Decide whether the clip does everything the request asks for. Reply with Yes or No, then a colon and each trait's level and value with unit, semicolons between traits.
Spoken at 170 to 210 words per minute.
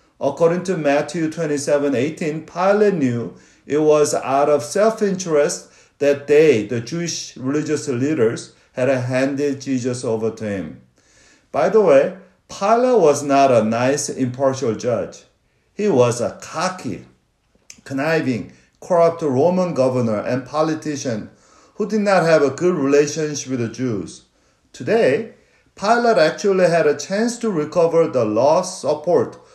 No: slow, 135 wpm